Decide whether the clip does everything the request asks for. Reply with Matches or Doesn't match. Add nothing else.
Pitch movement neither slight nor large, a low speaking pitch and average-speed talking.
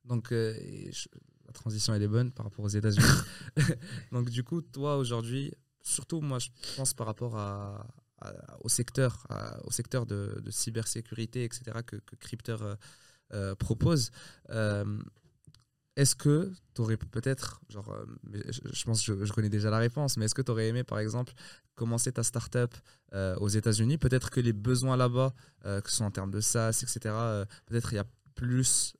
Matches